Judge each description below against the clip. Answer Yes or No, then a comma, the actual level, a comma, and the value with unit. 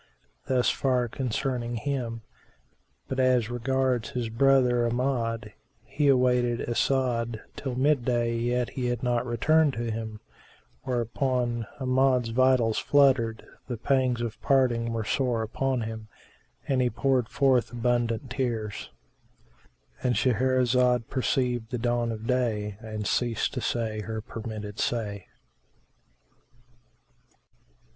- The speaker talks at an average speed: No, slow, 115 wpm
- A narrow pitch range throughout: Yes, narrow, 2.1 semitones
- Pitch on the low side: Yes, low, 120 Hz